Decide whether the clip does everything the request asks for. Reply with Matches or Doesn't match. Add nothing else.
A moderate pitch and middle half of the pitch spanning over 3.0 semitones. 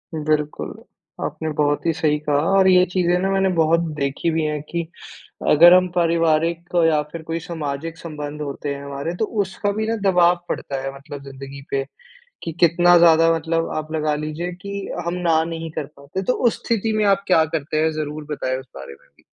Doesn't match